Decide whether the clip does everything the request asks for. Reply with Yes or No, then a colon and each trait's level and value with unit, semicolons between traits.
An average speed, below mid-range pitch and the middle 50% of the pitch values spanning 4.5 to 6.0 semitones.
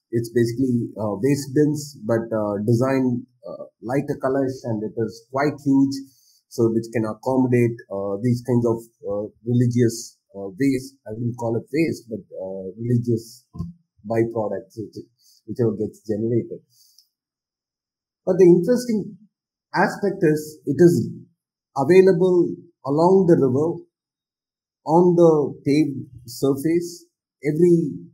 No: slow, 120 wpm; low, 130 Hz; average, 5.0 semitones